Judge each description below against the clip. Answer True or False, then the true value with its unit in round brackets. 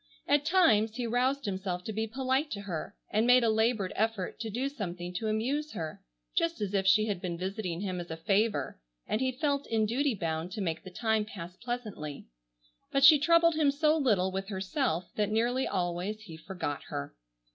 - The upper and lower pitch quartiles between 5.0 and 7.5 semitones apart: True (5.6 semitones)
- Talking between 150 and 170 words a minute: False (200 wpm)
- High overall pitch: True (215 Hz)